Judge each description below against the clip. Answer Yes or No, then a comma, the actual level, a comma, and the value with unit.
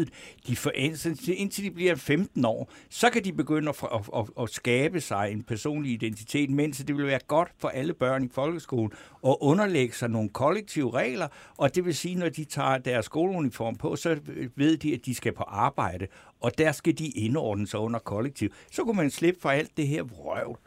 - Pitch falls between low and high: Yes, medium, 145 Hz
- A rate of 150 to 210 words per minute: Yes, average, 195 wpm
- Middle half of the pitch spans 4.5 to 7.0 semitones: Yes, average, 4.9 semitones